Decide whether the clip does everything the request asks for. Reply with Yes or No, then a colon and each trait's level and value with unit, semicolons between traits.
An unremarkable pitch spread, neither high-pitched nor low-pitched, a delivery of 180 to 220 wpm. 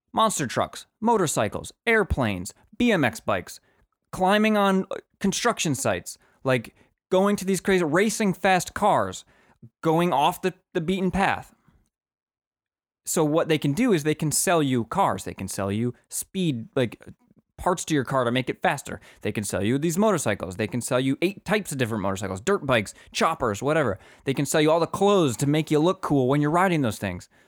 No: wide, 7.4 semitones; medium, 155 Hz; average, 185 wpm